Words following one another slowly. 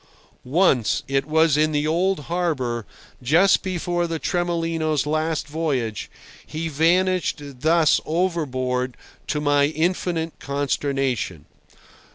Yes: slow, 95 wpm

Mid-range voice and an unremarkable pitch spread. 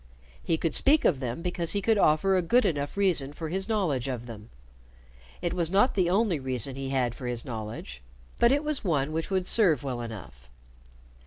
No: medium, 160 Hz; wide, 7.1 semitones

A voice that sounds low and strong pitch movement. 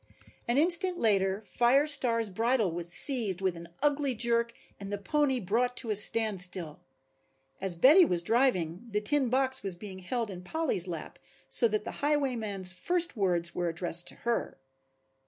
No: high, 220 Hz; wide, 5.9 semitones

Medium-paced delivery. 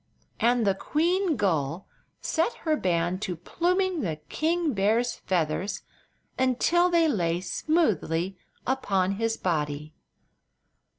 No: slow, 110 wpm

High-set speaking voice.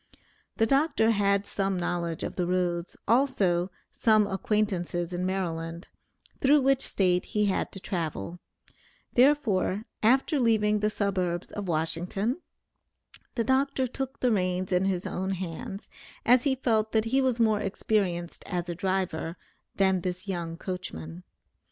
Yes: high, 195 Hz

